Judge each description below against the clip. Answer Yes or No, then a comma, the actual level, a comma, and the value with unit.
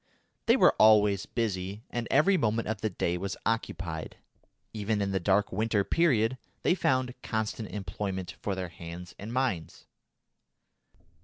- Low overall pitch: Yes, low, 105 Hz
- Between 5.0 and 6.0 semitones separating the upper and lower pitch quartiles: No, average, 3.2 semitones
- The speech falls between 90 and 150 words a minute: Yes, average, 145 wpm